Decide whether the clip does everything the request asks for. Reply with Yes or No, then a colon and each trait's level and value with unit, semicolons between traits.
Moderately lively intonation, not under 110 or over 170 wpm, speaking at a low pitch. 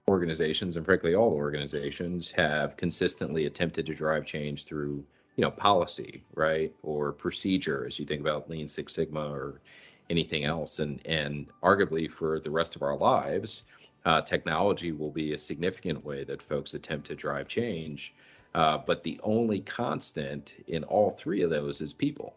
No: narrow, 1.8 semitones; average, 165 wpm; very low, 75 Hz